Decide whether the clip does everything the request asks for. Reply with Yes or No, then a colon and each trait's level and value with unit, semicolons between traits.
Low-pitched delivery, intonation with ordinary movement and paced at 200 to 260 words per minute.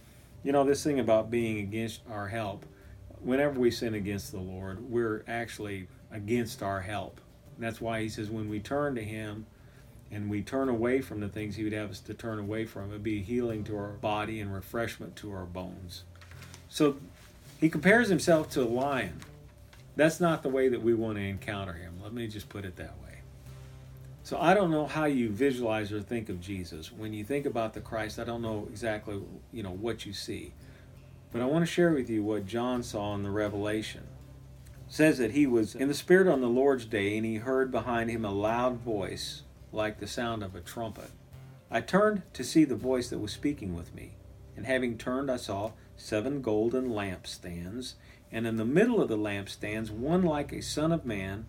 Yes: low, 110 Hz; average, 3.8 semitones; fast, 205 wpm